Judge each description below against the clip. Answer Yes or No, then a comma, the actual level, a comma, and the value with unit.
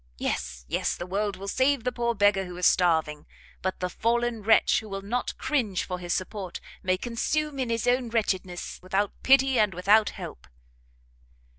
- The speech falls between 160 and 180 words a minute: Yes, average, 175 wpm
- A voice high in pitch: Yes, high, 205 Hz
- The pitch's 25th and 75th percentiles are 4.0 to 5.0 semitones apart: Yes, average, 4.6 semitones